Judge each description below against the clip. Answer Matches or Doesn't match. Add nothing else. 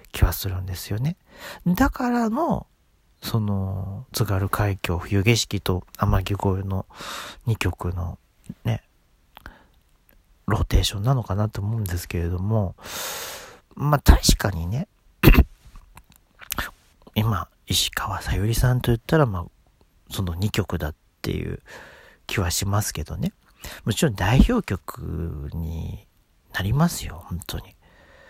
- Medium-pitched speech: Doesn't match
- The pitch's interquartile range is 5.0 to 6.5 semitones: Doesn't match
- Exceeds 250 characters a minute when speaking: Doesn't match